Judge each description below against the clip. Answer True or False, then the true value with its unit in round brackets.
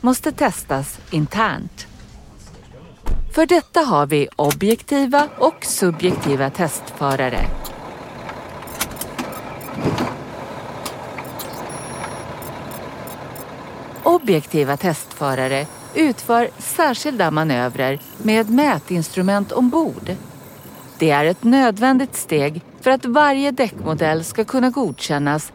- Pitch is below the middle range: False (185 Hz)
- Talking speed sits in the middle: False (75 wpm)